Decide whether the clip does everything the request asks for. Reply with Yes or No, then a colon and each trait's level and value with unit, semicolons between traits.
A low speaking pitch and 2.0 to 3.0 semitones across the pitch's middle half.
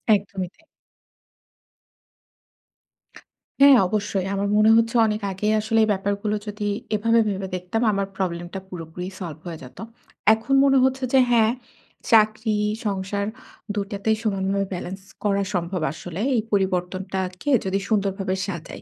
No: high, 200 Hz; narrow, 2.4 semitones